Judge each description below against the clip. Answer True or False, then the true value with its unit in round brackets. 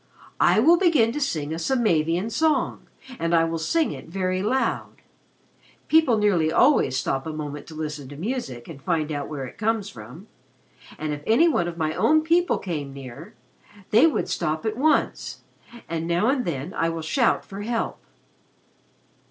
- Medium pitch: True (170 Hz)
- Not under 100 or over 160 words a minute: False (170 wpm)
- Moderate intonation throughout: False (7.4 semitones)